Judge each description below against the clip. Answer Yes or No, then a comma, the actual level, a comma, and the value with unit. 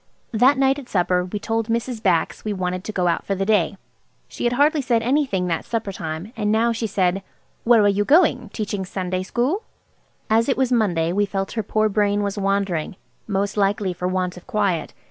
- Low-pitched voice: No, high, 205 Hz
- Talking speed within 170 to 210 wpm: Yes, fast, 205 wpm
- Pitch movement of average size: Yes, average, 3.7 semitones